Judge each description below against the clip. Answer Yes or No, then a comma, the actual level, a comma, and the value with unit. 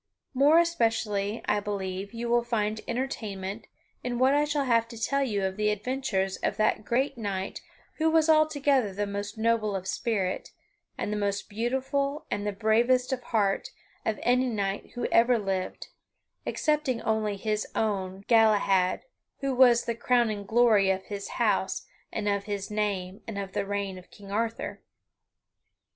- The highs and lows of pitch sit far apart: No, average, 3.6 semitones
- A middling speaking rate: Yes, average, 165 wpm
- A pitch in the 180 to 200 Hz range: No, high, 220 Hz